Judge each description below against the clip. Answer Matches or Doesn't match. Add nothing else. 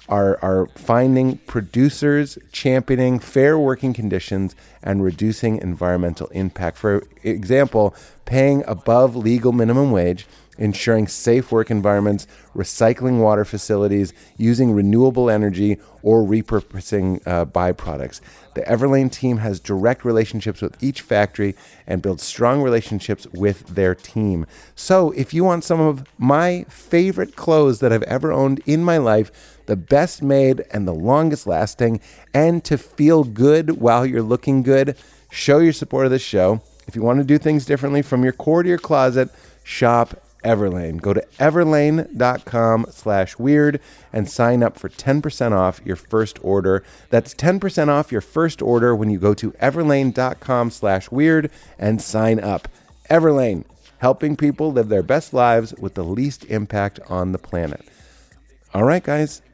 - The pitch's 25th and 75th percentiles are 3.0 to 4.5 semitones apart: Doesn't match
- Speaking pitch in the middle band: Doesn't match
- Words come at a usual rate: Matches